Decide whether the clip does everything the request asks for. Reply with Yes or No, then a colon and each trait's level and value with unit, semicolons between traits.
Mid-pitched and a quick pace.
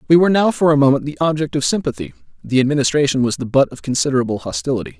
Yes: medium, 145 Hz; fast, 215 wpm